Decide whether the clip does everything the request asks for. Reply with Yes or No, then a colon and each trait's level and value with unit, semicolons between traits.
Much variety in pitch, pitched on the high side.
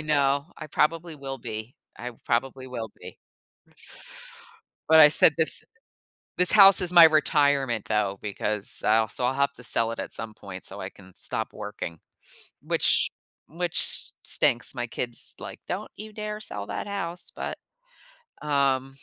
No: wide, 6.0 semitones; low, 135 Hz